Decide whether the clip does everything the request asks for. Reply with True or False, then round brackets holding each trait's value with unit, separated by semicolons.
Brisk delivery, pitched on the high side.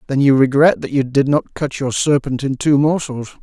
False (225 wpm; 140 Hz)